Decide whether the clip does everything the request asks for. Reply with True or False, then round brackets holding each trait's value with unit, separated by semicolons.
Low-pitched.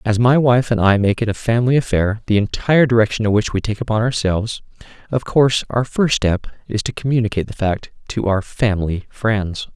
True (110 Hz)